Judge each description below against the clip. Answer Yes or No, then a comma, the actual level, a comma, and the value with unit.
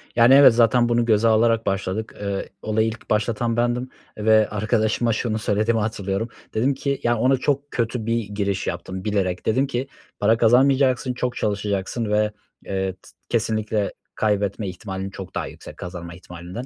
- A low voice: Yes, low, 110 Hz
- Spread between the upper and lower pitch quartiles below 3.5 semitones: Yes, average, 2.9 semitones